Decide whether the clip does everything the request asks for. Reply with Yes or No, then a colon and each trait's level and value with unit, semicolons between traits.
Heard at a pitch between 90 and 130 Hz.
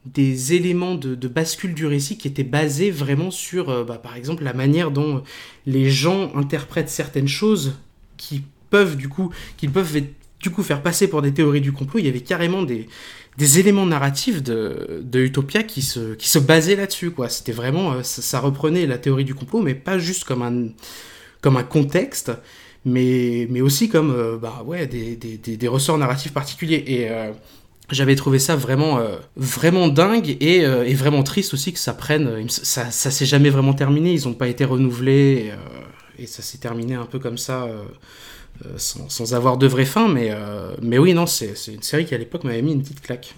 No: medium, 140 Hz